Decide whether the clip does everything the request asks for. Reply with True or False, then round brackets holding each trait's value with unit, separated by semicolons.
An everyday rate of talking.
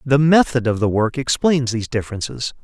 True (180 wpm)